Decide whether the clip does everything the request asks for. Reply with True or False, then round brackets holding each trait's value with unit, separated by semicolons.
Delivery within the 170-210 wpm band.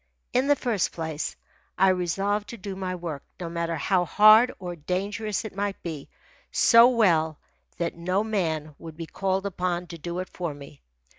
True (175 wpm)